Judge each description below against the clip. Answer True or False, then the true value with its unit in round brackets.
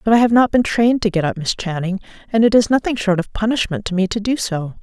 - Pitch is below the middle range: False (205 Hz)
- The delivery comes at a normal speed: False (285 wpm)